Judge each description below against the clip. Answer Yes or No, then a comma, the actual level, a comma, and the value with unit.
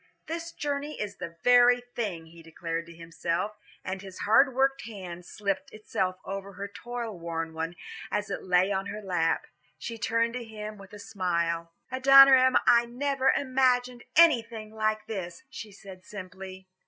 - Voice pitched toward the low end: No, high, 210 Hz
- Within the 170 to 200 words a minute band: No, average, 160 wpm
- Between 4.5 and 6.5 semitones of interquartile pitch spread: Yes, average, 5.0 semitones